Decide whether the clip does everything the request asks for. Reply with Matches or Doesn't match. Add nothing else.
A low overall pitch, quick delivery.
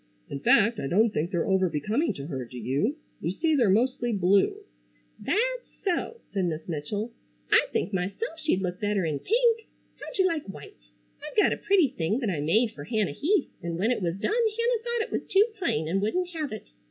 Doesn't match